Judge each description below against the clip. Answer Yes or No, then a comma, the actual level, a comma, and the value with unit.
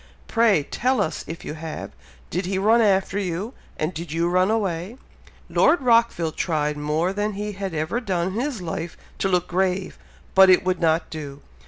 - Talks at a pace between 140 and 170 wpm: No, average, 185 wpm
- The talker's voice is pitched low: No, medium, 185 Hz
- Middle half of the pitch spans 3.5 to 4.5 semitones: Yes, average, 4.0 semitones